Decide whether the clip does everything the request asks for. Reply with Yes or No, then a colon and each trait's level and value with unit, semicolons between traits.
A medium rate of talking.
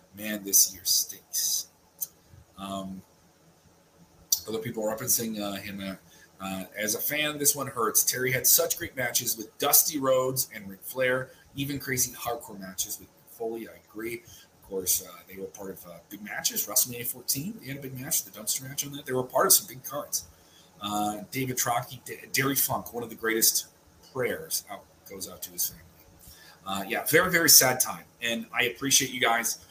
Yes: average, 190 wpm